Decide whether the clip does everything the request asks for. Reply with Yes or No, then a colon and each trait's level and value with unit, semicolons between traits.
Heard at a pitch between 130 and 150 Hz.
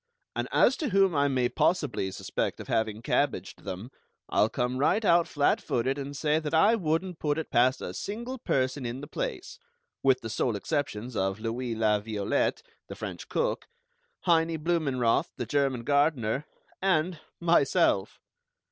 Yes: medium, 140 Hz